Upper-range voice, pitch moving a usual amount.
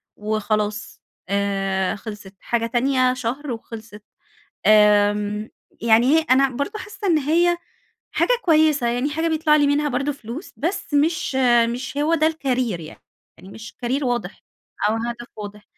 No: high, 245 Hz; wide, 5.7 semitones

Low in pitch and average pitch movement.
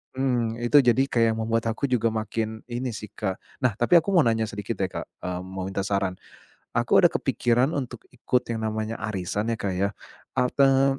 Yes: low, 115 Hz; average, 3.2 semitones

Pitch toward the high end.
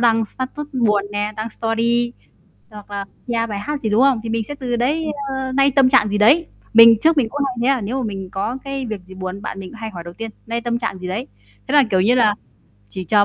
Yes: high, 230 Hz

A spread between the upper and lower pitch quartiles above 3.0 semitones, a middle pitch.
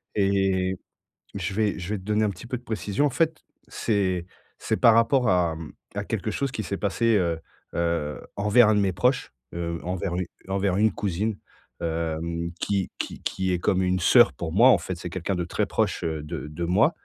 No: average, 3.7 semitones; very low, 95 Hz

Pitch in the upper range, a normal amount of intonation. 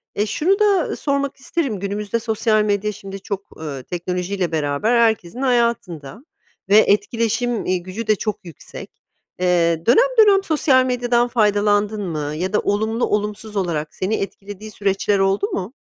Yes: high, 210 Hz; average, 4.2 semitones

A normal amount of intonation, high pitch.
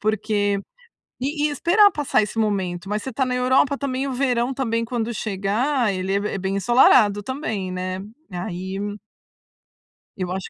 Yes: average, 5.0 semitones; high, 220 Hz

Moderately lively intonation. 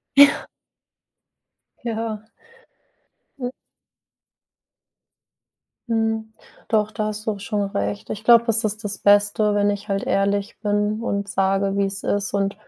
No: narrow, 1.6 semitones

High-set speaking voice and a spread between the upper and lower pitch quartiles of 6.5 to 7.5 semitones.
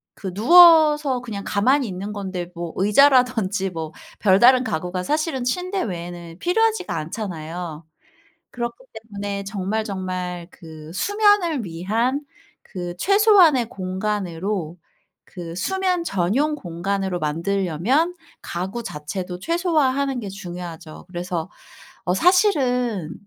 Yes: high, 200 Hz; wide, 7.2 semitones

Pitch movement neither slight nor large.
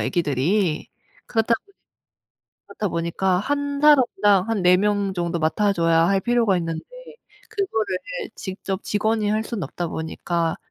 Yes: average, 4.5 semitones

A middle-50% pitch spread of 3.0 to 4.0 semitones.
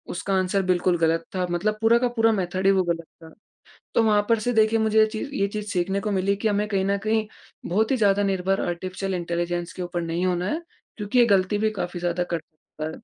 Yes: average, 3.3 semitones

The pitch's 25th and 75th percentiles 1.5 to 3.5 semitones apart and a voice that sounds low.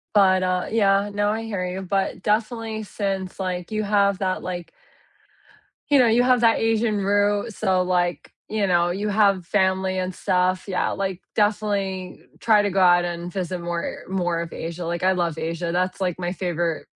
No: narrow, 2.5 semitones; high, 190 Hz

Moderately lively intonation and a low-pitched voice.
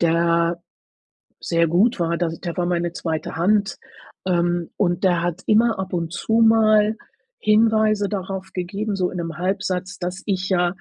No: average, 3.2 semitones; medium, 180 Hz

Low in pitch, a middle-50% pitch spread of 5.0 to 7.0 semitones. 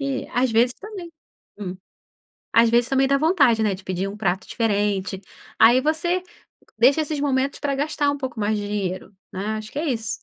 No: high, 235 Hz; average, 5.3 semitones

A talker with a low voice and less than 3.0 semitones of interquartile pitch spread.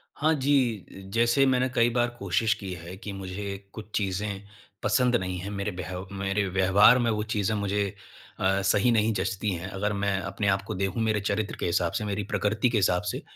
Yes: low, 100 Hz; narrow, 2.4 semitones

